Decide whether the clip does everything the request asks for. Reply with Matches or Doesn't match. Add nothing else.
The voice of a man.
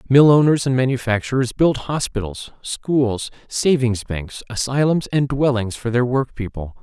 Matches